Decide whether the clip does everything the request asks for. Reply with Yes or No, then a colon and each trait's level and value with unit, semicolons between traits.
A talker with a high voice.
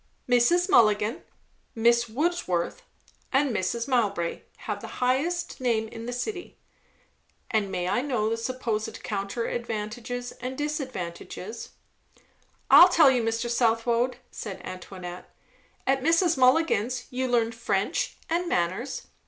Yes: high, 240 Hz